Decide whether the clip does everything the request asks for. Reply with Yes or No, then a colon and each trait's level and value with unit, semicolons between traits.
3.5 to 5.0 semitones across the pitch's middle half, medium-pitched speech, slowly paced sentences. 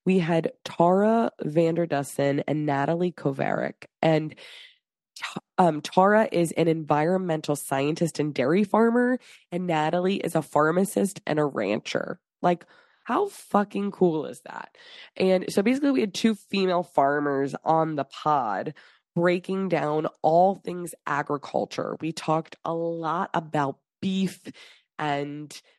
Yes: average, 4.1 semitones; medium, 170 Hz; slow, 125 wpm